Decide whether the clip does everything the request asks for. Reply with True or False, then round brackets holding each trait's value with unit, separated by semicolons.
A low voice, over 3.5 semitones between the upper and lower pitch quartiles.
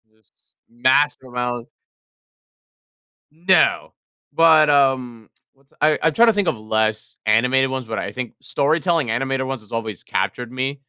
True (130 Hz; 4.1 semitones)